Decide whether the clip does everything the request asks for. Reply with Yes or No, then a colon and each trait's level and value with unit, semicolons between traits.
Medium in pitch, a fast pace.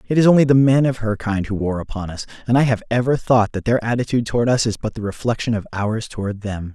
No: low, 115 Hz; fast, 265 wpm